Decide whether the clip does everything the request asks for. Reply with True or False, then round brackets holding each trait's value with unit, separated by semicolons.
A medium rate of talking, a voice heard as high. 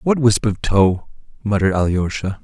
False (150 wpm; 105 Hz)